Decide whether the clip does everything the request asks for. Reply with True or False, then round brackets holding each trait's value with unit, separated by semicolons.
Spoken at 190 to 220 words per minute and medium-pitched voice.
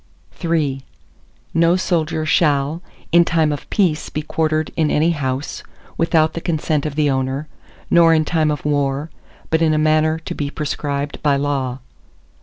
False (165 wpm; 155 Hz)